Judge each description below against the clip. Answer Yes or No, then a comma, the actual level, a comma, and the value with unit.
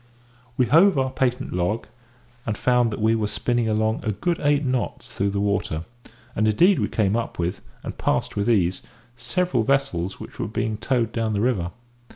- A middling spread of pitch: Yes, average, 4.0 semitones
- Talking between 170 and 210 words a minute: Yes, average, 190 wpm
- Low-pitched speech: Yes, low, 110 Hz